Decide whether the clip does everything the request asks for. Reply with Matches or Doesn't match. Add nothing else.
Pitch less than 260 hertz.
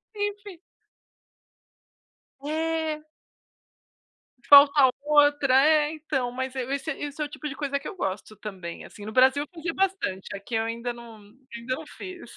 Doesn't match